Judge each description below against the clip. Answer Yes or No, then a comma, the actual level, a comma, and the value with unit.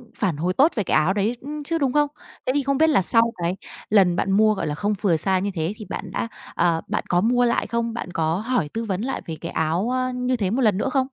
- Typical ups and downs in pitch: No, wide, 5.8 semitones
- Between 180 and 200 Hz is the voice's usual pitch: No, high, 215 Hz